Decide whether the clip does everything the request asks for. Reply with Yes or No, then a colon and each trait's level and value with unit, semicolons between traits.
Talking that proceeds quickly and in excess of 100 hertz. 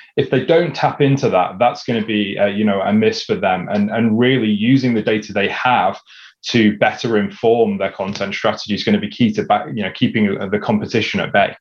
Yes: fast, 235 wpm; low, 130 Hz